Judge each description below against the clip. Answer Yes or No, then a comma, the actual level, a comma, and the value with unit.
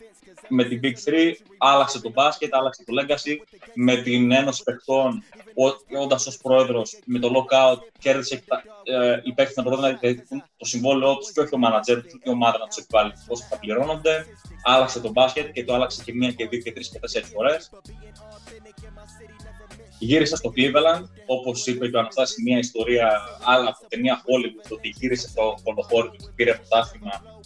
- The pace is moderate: No, fast, 180 wpm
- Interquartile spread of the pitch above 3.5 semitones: No, average, 2.8 semitones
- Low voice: Yes, low, 125 Hz